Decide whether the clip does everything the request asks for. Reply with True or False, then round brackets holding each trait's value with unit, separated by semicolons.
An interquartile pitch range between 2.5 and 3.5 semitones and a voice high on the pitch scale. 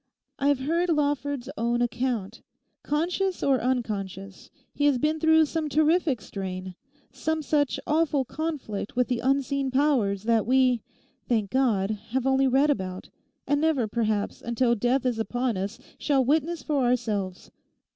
False (4.6 semitones; 260 Hz)